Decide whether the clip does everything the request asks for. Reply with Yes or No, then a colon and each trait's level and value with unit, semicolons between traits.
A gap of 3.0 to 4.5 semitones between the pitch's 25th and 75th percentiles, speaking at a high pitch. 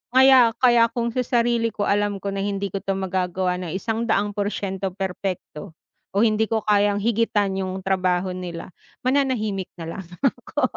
Yes: average, 3.3 semitones; high, 200 Hz